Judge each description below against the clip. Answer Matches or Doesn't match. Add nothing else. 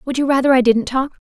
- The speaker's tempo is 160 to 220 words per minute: Doesn't match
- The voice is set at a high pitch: Matches